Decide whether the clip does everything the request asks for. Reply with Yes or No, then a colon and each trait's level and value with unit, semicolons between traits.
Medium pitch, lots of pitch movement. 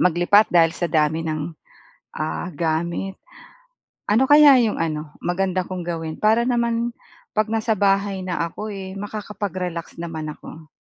No: medium, 180 Hz; average, 4.5 semitones